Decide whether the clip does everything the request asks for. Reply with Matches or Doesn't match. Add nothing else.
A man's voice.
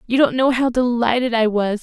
Doesn't match